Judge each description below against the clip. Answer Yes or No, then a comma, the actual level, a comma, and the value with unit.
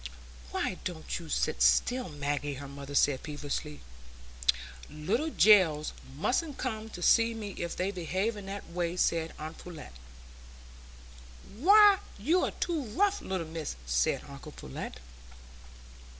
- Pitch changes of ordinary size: No, wide, 7.1 semitones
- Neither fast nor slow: No, slow, 130 wpm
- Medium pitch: Yes, medium, 180 Hz